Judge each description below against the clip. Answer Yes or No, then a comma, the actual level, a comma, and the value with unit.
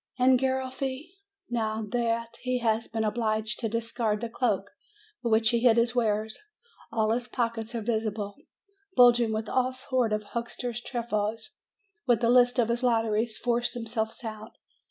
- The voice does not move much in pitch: Yes, narrow, 1.9 semitones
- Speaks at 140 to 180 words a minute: Yes, average, 165 wpm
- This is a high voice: Yes, high, 230 Hz